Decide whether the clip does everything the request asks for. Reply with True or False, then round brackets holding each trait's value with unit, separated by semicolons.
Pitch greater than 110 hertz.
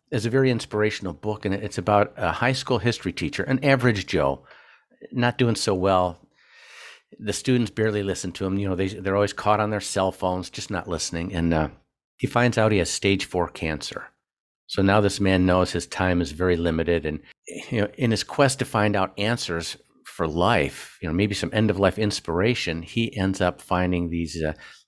False (100 Hz)